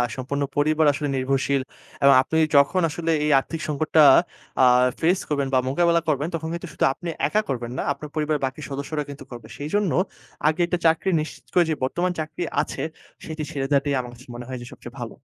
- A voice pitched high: No, medium, 150 Hz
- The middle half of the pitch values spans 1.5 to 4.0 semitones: Yes, average, 2.9 semitones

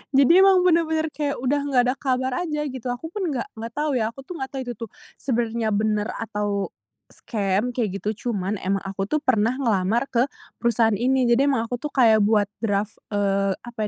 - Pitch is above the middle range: Yes, high, 235 Hz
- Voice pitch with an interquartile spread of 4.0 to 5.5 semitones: Yes, average, 4.5 semitones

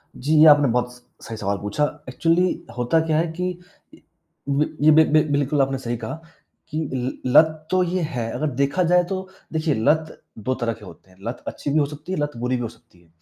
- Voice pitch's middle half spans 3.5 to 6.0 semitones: Yes, average, 4.5 semitones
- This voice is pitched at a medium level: Yes, medium, 145 Hz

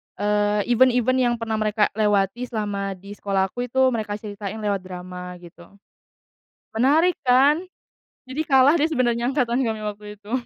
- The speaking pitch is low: No, high, 220 Hz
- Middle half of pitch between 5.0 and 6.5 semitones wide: No, average, 3.7 semitones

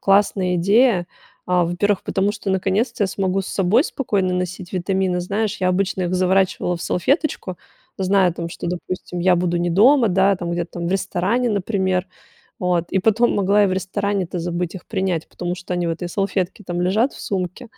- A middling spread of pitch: No, narrow, 2.1 semitones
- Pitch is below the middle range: No, medium, 185 Hz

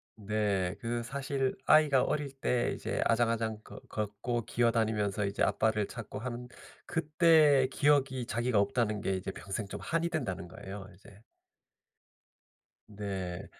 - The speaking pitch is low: Yes, low, 115 Hz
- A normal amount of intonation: Yes, average, 4.6 semitones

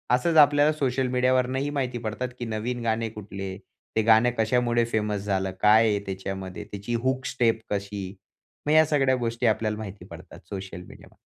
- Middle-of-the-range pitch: No, low, 115 Hz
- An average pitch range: Yes, average, 3.8 semitones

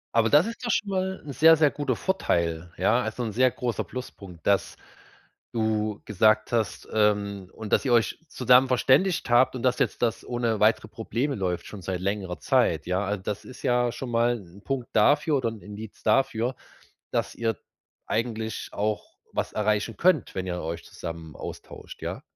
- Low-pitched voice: Yes, low, 110 Hz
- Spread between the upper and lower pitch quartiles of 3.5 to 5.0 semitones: Yes, average, 3.9 semitones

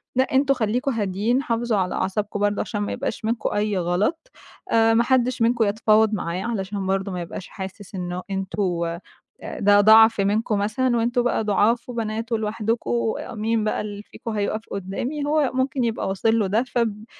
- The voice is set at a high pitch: Yes, high, 215 Hz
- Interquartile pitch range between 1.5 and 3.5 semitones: Yes, average, 2.9 semitones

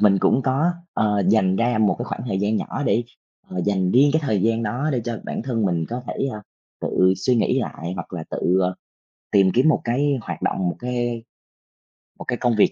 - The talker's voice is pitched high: No, low, 110 Hz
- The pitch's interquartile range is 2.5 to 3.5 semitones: No, average, 4.5 semitones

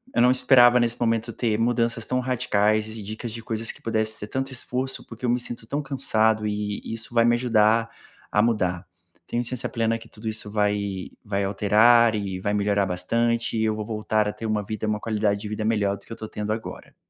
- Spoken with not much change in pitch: Yes, narrow, 2.1 semitones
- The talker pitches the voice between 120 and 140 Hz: No, low, 110 Hz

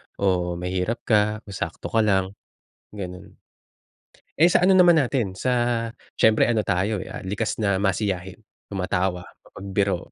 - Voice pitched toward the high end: No, low, 100 Hz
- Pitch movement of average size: Yes, average, 3.2 semitones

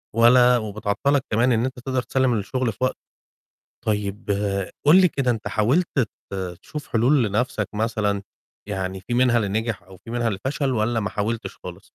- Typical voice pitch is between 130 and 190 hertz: No, low, 115 Hz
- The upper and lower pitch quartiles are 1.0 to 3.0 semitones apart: No, average, 3.5 semitones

